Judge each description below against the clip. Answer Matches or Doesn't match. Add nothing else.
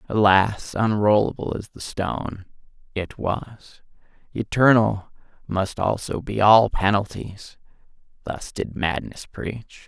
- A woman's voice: Doesn't match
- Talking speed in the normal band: Doesn't match